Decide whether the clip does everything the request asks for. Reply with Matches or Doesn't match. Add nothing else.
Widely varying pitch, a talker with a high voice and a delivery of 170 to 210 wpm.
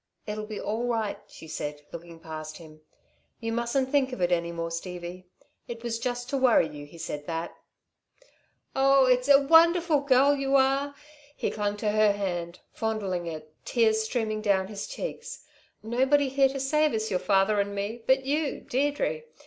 Matches